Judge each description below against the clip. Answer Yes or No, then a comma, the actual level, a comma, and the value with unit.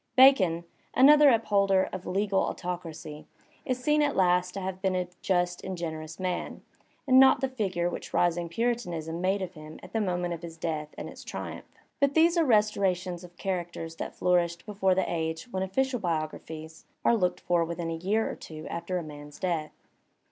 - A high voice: No, medium, 180 Hz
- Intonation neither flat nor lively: Yes, average, 3.8 semitones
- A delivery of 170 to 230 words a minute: Yes, average, 190 wpm